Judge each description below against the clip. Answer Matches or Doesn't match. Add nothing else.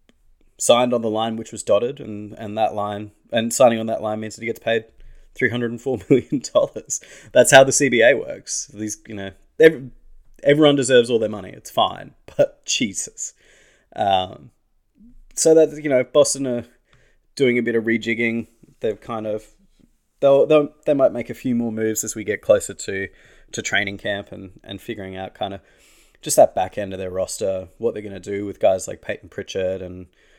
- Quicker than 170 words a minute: Matches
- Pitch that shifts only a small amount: Doesn't match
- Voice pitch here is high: Doesn't match